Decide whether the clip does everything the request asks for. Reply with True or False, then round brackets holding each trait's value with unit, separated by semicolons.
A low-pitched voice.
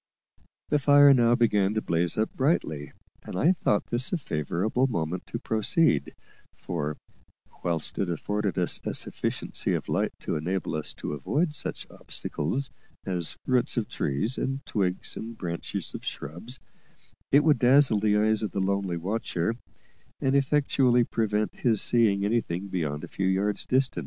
True (105 Hz)